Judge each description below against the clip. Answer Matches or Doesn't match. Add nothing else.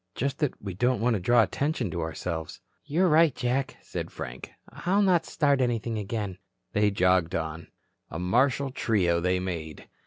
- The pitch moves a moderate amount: Doesn't match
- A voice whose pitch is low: Matches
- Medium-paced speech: Matches